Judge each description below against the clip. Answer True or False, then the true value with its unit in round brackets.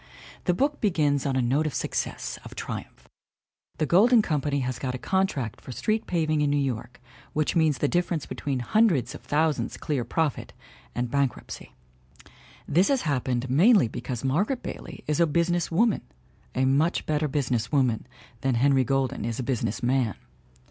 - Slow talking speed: False (170 wpm)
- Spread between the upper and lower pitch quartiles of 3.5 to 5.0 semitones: True (4.6 semitones)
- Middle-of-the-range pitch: True (145 Hz)